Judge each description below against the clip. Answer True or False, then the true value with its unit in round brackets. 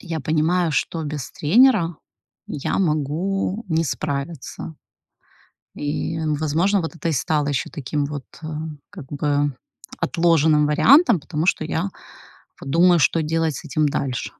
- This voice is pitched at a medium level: True (155 Hz)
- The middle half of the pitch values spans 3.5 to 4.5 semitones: False (2.7 semitones)